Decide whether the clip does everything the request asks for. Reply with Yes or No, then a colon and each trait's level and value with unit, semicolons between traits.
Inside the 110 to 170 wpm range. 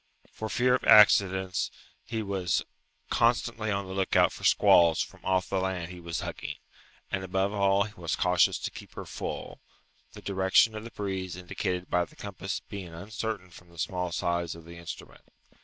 No: average, 180 wpm